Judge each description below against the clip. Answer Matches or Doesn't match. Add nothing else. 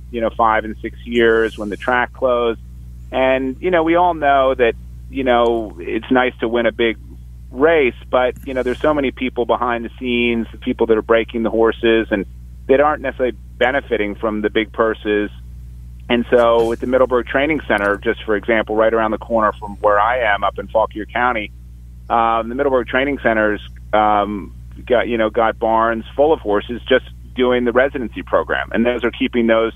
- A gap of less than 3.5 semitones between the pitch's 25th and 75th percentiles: Matches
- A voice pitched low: Matches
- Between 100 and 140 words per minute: Doesn't match